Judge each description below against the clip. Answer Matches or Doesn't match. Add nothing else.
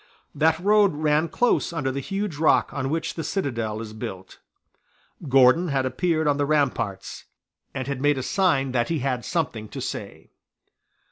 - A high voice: Doesn't match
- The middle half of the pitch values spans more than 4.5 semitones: Doesn't match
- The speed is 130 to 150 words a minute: Doesn't match